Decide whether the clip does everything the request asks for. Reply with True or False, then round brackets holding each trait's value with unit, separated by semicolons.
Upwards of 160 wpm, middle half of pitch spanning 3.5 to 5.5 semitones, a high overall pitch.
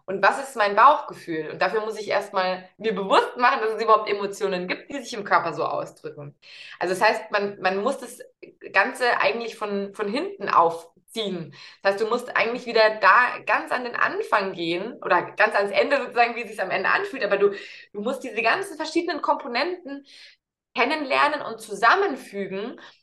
True (185 wpm; 4.5 semitones; 215 Hz)